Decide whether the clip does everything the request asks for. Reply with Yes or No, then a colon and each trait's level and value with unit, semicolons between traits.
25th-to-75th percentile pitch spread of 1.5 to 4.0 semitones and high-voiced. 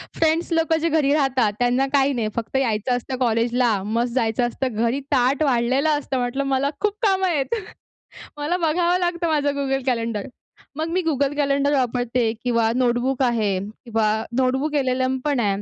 Yes: average, 3.7 semitones; very high, 265 Hz